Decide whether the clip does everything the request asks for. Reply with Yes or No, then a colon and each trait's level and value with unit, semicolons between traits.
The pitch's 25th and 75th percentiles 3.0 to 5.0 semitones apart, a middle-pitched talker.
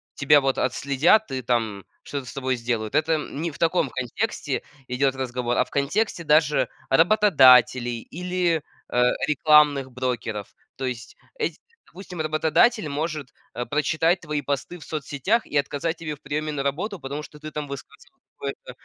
Yes: average, 3.8 semitones; medium, 145 Hz